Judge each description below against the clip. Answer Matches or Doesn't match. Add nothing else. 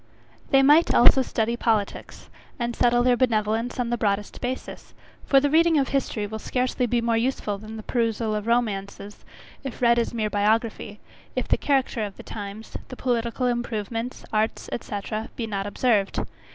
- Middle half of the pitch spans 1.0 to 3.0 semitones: Matches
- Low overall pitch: Doesn't match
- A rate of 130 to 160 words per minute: Doesn't match